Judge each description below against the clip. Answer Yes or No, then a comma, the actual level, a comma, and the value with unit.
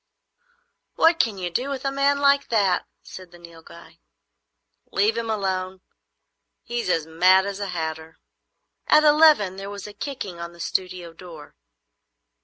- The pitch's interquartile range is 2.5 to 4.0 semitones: No, wide, 5.5 semitones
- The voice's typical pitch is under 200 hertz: Yes, high, 190 Hz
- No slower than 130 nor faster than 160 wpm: Yes, average, 150 wpm